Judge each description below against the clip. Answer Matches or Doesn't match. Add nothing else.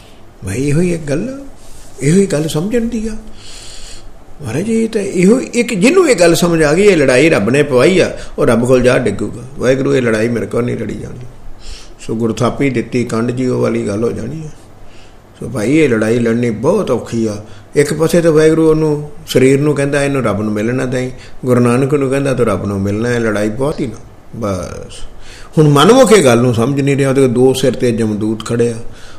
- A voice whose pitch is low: Matches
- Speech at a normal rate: Doesn't match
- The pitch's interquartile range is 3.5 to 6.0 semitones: Matches